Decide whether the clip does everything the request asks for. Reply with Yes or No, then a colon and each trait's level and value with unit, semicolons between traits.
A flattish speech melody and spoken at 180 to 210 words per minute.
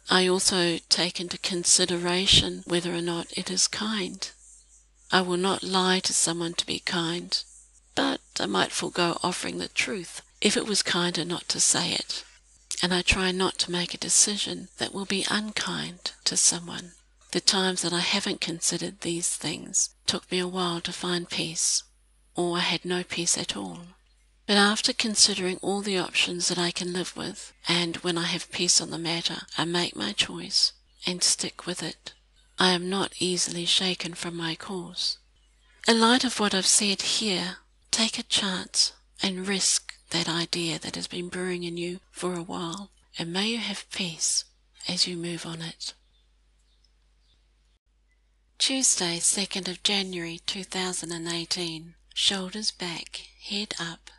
No: narrow, 2.0 semitones; average, 170 wpm